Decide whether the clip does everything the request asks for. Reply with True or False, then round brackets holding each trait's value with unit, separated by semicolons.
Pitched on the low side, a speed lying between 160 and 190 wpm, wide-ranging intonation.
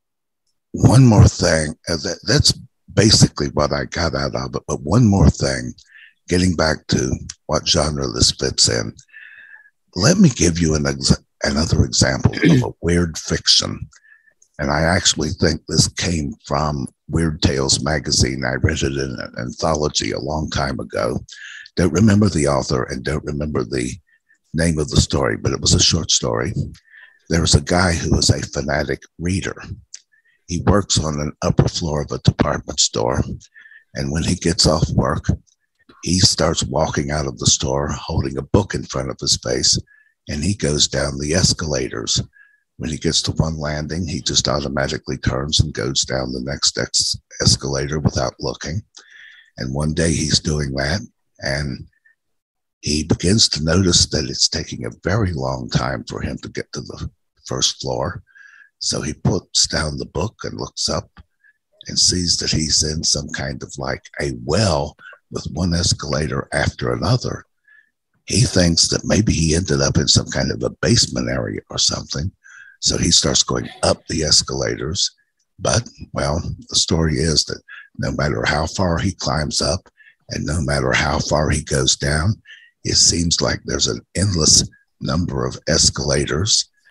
True (80 Hz; 165 wpm; 6.3 semitones)